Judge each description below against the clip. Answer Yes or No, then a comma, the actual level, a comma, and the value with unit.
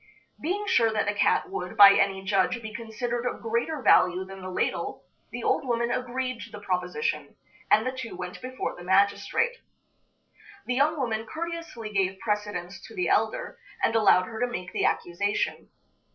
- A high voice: Yes, high, 220 Hz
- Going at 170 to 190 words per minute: Yes, average, 175 wpm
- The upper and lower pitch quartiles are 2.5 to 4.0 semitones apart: No, average, 4.7 semitones